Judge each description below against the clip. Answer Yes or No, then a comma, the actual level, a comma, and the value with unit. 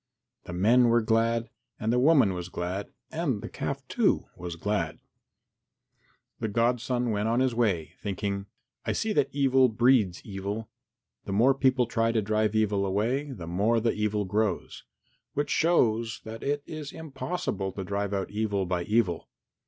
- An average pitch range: Yes, average, 3.8 semitones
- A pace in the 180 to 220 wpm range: No, average, 160 wpm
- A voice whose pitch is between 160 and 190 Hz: No, low, 110 Hz